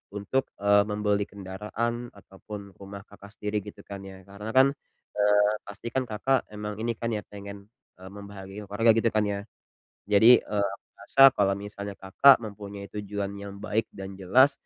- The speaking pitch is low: Yes, low, 105 Hz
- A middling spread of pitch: No, narrow, 1.4 semitones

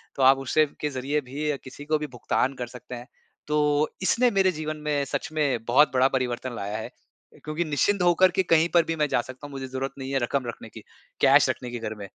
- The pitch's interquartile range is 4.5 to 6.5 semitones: No, average, 3.4 semitones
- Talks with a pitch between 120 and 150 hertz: Yes, low, 135 Hz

